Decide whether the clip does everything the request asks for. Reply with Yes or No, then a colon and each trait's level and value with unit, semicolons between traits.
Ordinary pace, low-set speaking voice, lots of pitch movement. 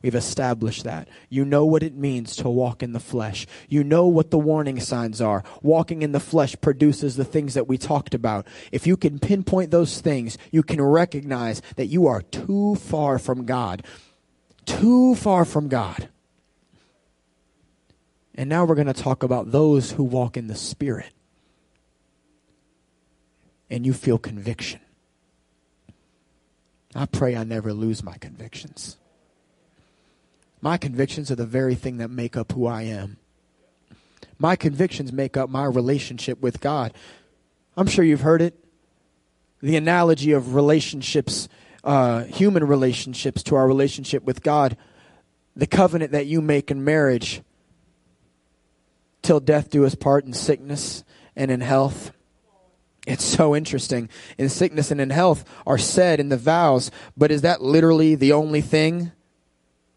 Yes: average, 150 wpm; low, 130 Hz; wide, 6.0 semitones